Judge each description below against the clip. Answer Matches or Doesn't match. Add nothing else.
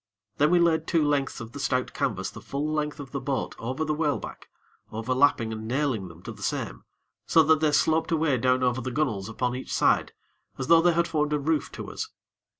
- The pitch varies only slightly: Doesn't match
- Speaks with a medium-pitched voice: Matches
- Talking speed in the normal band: Doesn't match